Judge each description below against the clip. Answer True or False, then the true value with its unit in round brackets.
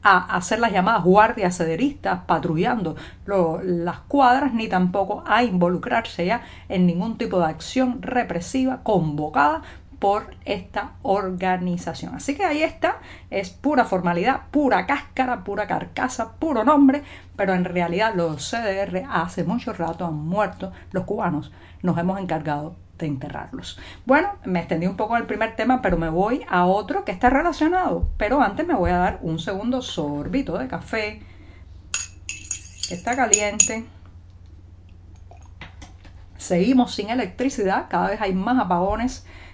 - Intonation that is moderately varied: False (6.1 semitones)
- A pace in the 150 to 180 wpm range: False (140 wpm)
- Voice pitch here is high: True (195 Hz)